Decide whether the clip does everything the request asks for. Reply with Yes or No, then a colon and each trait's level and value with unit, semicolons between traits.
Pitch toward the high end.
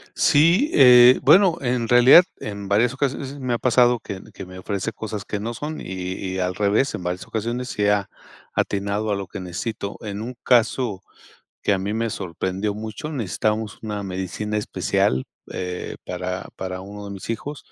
No: low, 105 Hz